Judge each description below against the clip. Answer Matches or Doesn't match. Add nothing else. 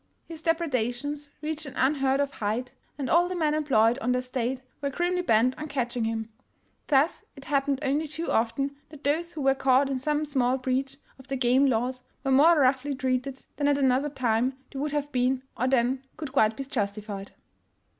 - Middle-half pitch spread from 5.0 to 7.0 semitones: Doesn't match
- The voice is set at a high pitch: Matches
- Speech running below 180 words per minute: Doesn't match